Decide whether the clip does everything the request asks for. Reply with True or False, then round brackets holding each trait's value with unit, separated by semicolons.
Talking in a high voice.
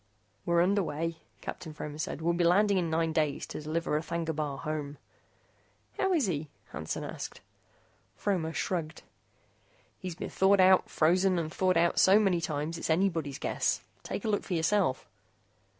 False (165 Hz)